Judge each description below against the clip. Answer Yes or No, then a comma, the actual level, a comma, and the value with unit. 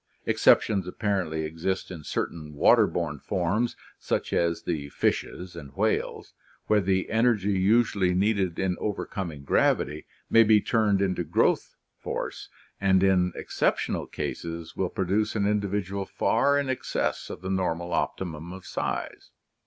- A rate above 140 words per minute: No, slow, 135 wpm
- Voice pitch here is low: Yes, very low, 95 Hz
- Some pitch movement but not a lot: Yes, average, 3.3 semitones